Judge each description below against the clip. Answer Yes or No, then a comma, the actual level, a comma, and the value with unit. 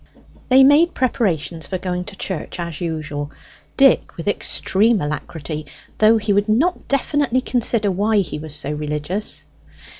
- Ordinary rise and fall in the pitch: No, wide, 6.8 semitones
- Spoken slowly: No, average, 145 wpm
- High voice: Yes, high, 195 Hz